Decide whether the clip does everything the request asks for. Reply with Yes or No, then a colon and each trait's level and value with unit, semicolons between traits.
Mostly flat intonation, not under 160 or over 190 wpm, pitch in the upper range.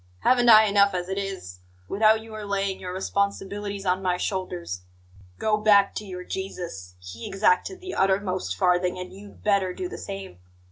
Yes: narrow, 2.2 semitones; average, 170 wpm; high, 195 Hz